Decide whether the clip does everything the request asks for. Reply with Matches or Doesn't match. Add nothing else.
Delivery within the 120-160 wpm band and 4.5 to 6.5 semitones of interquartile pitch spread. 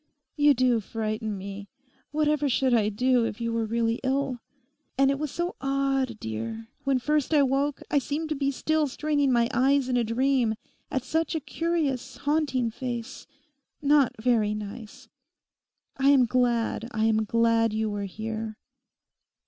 Doesn't match